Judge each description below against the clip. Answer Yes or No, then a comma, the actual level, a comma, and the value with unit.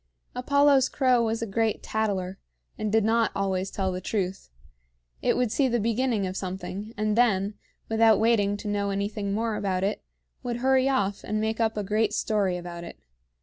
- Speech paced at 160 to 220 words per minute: Yes, average, 185 wpm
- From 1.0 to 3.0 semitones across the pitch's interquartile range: Yes, average, 2.7 semitones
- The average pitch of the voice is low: No, high, 215 Hz